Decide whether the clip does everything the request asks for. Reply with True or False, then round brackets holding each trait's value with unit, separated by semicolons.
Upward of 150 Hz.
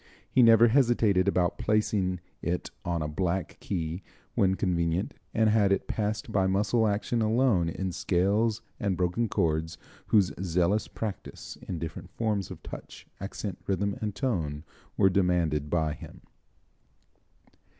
False (95 Hz)